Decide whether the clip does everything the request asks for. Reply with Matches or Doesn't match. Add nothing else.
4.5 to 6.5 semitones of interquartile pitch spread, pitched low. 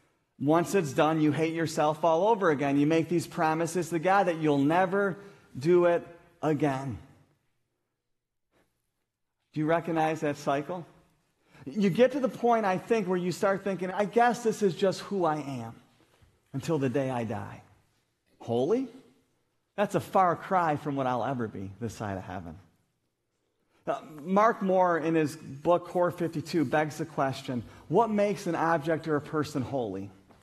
Doesn't match